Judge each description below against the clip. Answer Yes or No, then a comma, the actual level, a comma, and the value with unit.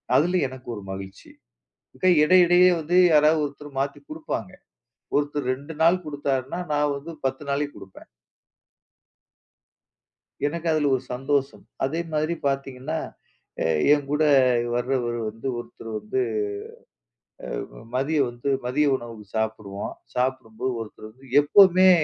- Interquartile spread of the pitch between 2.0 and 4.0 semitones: Yes, average, 3.7 semitones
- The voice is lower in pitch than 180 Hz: Yes, medium, 140 Hz